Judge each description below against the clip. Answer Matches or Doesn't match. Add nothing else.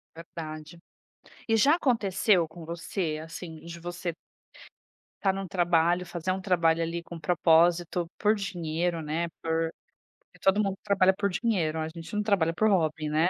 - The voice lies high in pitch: Doesn't match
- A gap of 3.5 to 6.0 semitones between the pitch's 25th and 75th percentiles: Doesn't match